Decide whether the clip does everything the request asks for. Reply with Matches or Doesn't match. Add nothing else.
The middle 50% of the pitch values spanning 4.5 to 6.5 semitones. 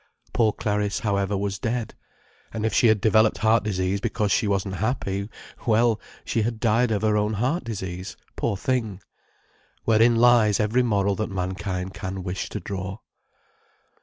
Doesn't match